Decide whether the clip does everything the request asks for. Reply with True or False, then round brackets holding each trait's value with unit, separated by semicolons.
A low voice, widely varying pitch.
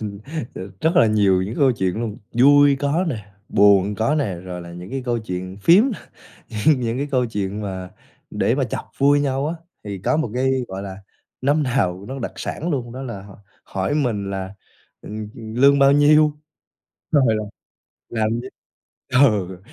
True (115 Hz; 5.9 semitones)